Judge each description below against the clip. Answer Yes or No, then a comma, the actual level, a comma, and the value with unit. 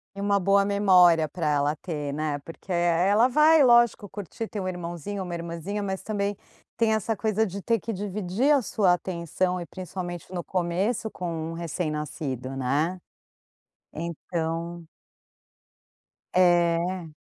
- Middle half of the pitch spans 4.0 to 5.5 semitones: No, average, 3.4 semitones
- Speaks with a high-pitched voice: No, medium, 180 Hz